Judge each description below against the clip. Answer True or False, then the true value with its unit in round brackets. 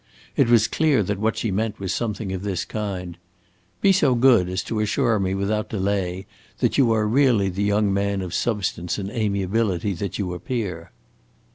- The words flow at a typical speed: True (180 wpm)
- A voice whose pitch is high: False (100 Hz)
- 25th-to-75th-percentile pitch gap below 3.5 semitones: True (2.9 semitones)